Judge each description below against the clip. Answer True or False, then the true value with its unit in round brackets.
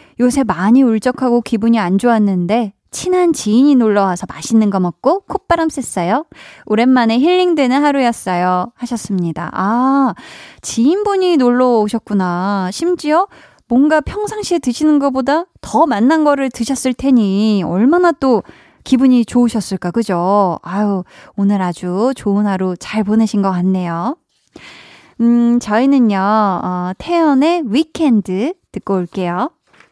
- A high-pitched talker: True (235 Hz)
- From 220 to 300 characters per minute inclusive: True (280 characters per minute)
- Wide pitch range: True (5.8 semitones)